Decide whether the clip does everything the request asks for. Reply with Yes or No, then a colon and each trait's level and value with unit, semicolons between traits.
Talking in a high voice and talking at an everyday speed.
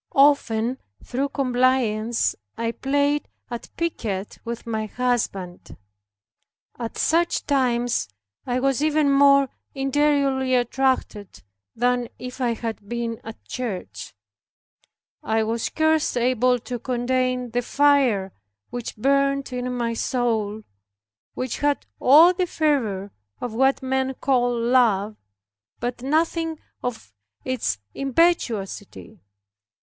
No: very high, 250 Hz; slow, 110 wpm